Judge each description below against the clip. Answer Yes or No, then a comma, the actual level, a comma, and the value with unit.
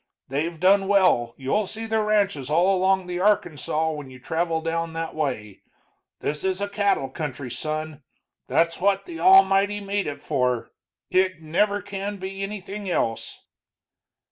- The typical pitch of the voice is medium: Yes, medium, 180 Hz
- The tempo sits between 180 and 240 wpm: No, average, 150 wpm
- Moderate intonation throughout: Yes, average, 4.7 semitones